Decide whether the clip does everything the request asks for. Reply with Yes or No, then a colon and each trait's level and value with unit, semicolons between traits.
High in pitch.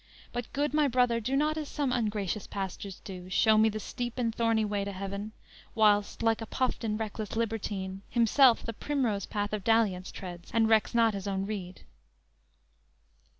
Yes: high, 220 Hz